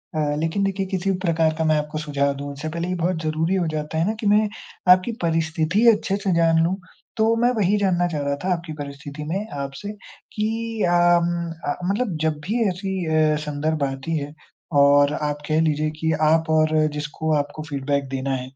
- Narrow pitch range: No, average, 4.0 semitones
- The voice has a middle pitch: Yes, medium, 160 Hz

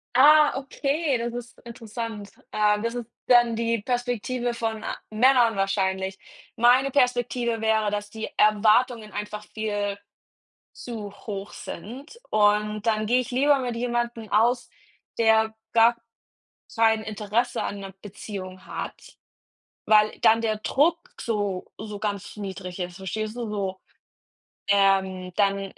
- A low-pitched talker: No, high, 220 Hz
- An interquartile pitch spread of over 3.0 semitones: No, average, 2.7 semitones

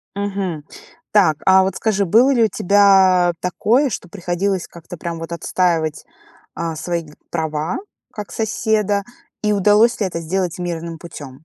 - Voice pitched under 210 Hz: Yes, medium, 185 Hz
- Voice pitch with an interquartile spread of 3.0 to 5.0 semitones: Yes, average, 3.3 semitones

